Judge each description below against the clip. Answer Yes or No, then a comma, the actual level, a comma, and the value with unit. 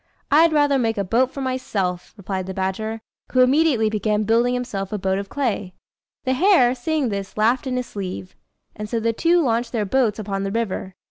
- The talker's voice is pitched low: No, high, 225 Hz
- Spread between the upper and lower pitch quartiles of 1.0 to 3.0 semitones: No, average, 4.5 semitones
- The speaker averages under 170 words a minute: No, average, 200 wpm